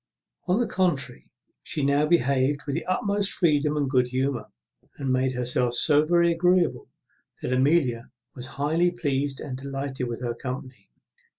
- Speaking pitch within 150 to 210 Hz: No, medium, 140 Hz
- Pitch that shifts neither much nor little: Yes, average, 4.3 semitones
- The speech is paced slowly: No, average, 155 wpm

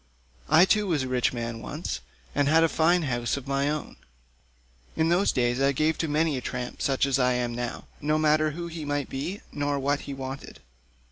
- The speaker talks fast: Yes, fast, 210 wpm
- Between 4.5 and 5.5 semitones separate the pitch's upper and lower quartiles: No, average, 3.3 semitones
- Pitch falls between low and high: Yes, medium, 145 Hz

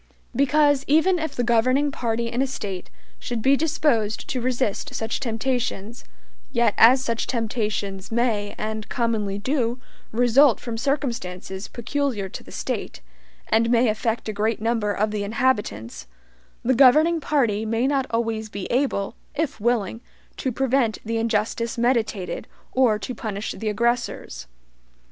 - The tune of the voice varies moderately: Yes, average, 3.3 semitones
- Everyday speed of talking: Yes, average, 145 wpm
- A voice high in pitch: Yes, high, 230 Hz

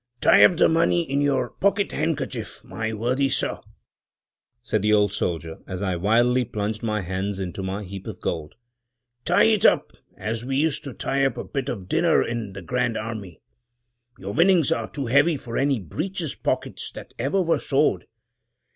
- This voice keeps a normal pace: Yes, average, 180 wpm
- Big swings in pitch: Yes, wide, 6.0 semitones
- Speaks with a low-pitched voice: Yes, low, 120 Hz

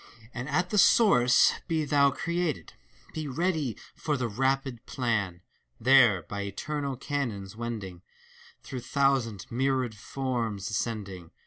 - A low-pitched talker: Yes, low, 125 Hz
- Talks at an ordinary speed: No, slow, 120 wpm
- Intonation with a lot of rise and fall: No, average, 4.8 semitones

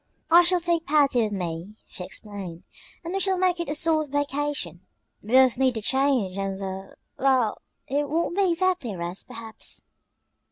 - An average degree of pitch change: No, wide, 8.8 semitones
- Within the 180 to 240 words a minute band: Yes, average, 185 wpm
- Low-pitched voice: No, very high, 265 Hz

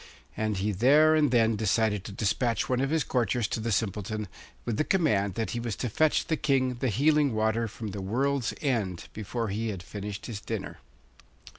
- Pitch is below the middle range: Yes, low, 115 Hz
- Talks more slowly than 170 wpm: No, average, 195 wpm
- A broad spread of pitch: No, average, 3.9 semitones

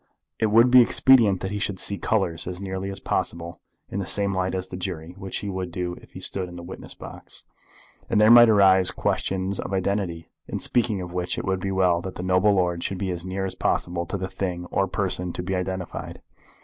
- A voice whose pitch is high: No, very low, 95 Hz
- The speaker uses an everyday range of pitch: No, narrow, 1.7 semitones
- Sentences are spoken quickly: Yes, fast, 230 wpm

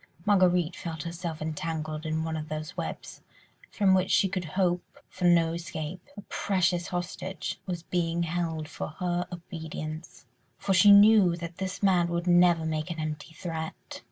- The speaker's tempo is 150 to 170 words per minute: Yes, average, 160 wpm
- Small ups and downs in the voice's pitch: Yes, narrow, 2.1 semitones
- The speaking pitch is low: No, medium, 170 Hz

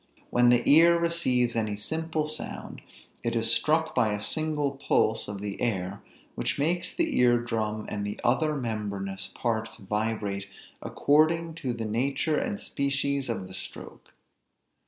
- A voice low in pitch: Yes, low, 120 Hz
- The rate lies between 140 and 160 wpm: Yes, average, 150 wpm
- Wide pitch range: Yes, wide, 6.3 semitones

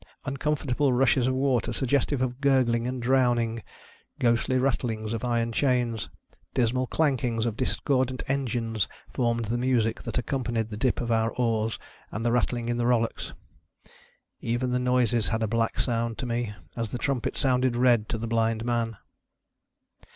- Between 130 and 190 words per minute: Yes, average, 160 wpm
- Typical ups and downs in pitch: No, narrow, 2.0 semitones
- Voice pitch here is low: Yes, low, 120 Hz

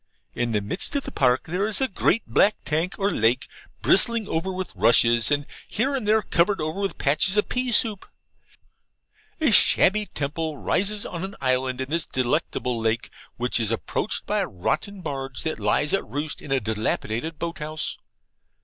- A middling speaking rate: Yes, average, 175 wpm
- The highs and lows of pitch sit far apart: Yes, wide, 7.9 semitones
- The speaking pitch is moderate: Yes, medium, 155 Hz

